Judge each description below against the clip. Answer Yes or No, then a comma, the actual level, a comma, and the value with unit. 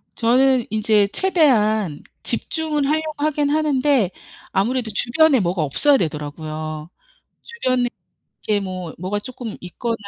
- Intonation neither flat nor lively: No, wide, 7.6 semitones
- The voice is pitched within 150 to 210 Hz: No, high, 230 Hz